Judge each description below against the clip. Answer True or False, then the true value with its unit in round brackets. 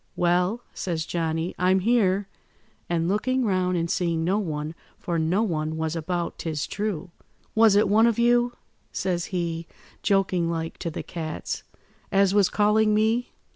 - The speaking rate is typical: True (155 wpm)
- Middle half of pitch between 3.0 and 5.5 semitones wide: True (4.1 semitones)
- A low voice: False (180 Hz)